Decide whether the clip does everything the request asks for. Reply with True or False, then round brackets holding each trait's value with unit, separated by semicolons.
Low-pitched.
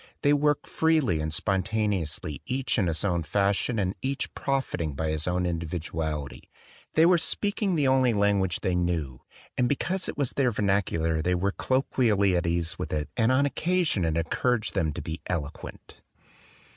True (95 Hz)